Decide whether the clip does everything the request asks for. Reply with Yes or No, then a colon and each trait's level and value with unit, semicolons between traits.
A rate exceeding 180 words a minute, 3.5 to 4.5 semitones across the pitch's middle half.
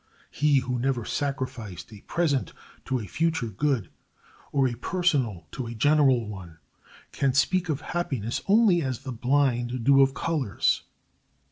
No: average, 145 wpm; average, 3.9 semitones